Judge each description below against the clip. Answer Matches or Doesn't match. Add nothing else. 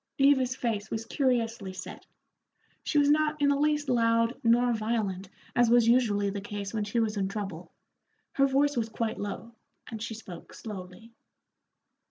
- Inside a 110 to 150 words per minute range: Doesn't match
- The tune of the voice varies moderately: Matches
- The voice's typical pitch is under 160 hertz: Doesn't match